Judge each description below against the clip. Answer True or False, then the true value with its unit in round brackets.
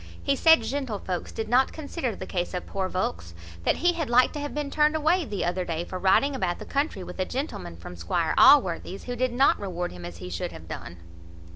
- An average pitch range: False (8.1 semitones)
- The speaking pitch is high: True (205 Hz)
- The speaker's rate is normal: False (230 wpm)